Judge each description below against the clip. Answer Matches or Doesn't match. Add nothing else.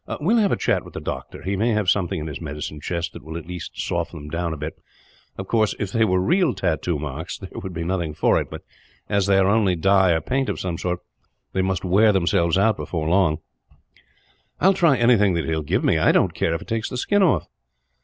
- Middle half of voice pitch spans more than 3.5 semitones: Matches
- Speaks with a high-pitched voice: Doesn't match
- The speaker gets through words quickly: Matches